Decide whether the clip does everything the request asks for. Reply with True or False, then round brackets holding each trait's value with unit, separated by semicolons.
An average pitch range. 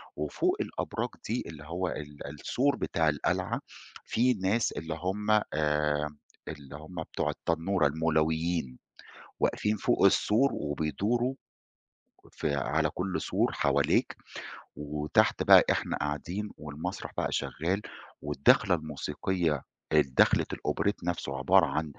True (4.2 semitones)